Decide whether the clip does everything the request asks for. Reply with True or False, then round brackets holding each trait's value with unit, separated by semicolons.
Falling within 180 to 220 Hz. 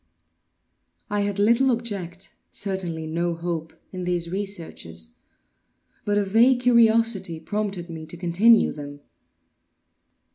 True (190 Hz)